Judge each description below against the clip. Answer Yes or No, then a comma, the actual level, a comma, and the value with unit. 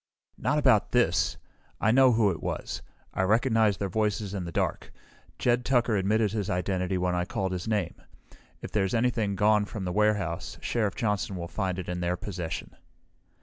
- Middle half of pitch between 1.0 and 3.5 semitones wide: Yes, average, 3.2 semitones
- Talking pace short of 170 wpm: No, average, 180 wpm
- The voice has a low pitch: Yes, low, 100 Hz